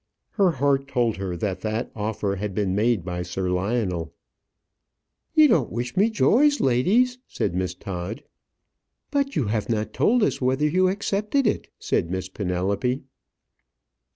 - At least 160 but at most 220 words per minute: No, average, 150 wpm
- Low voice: Yes, low, 115 Hz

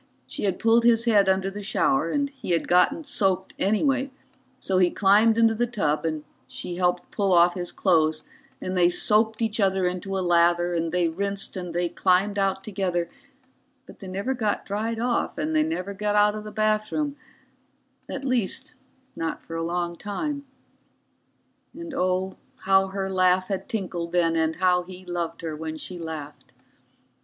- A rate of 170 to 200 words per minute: Yes, average, 175 wpm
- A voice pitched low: No, high, 190 Hz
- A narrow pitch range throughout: No, average, 3.5 semitones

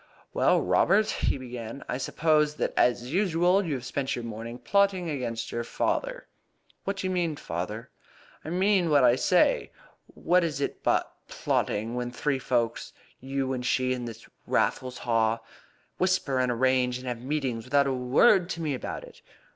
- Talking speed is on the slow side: No, average, 170 wpm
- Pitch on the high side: No, low, 130 Hz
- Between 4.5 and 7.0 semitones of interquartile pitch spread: Yes, wide, 5.4 semitones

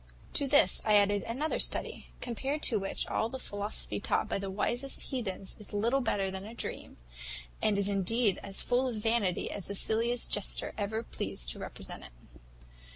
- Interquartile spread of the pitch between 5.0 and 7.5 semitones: No, average, 3.4 semitones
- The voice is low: No, high, 215 Hz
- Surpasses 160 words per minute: Yes, average, 180 wpm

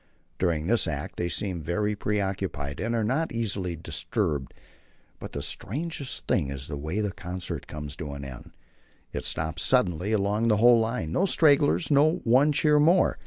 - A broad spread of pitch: Yes, wide, 7.3 semitones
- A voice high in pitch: No, low, 100 Hz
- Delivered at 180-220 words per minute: No, average, 170 wpm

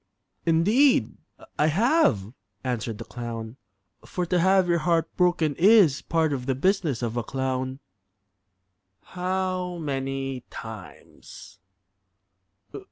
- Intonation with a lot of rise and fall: Yes, wide, 5.9 semitones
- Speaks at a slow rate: Yes, slow, 105 wpm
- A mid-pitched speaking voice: Yes, medium, 155 Hz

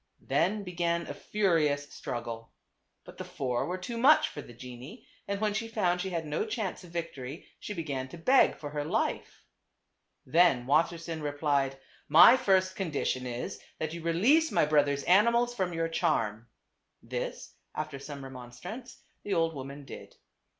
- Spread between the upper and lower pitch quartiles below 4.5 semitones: No, wide, 5.4 semitones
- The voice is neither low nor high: Yes, medium, 165 Hz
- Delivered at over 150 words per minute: Yes, average, 165 wpm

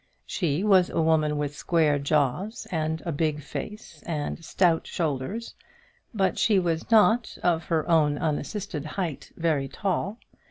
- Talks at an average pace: Yes, average, 145 wpm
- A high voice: No, medium, 160 Hz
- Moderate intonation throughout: Yes, average, 4.1 semitones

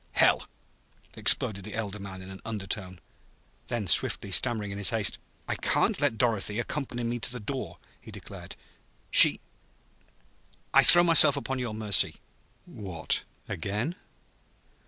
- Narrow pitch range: No, average, 3.5 semitones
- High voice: No, low, 105 Hz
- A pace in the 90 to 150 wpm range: Yes, average, 140 wpm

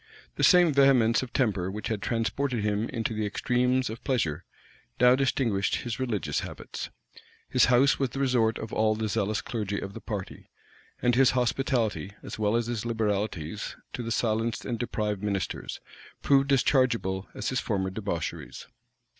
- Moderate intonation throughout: Yes, average, 3.3 semitones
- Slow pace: No, average, 165 wpm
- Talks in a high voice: No, low, 115 Hz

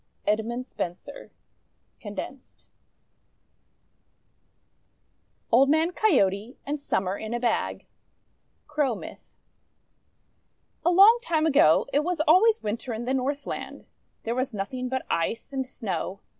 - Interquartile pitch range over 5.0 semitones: Yes, wide, 5.4 semitones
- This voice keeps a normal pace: No, slow, 115 wpm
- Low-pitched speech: No, very high, 255 Hz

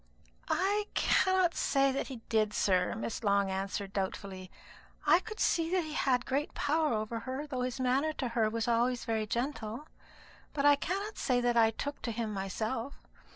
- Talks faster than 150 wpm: Yes, average, 180 wpm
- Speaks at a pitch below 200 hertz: No, high, 245 Hz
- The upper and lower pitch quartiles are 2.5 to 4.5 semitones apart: No, average, 5.1 semitones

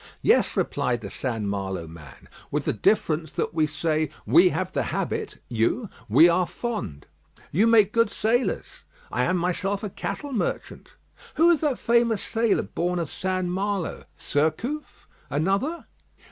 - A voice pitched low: No, medium, 185 Hz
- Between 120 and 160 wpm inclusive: Yes, average, 150 wpm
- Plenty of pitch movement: Yes, wide, 7.2 semitones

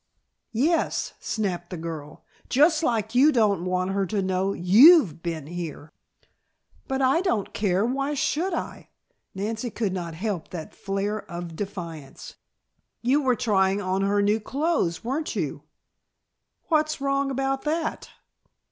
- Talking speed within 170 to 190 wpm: No, average, 140 wpm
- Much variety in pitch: Yes, wide, 7.0 semitones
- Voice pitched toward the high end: Yes, high, 205 Hz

